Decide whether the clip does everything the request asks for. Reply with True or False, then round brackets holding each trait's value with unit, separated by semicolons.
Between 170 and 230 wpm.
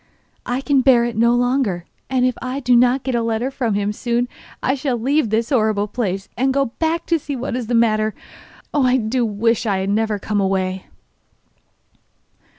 True (195 wpm)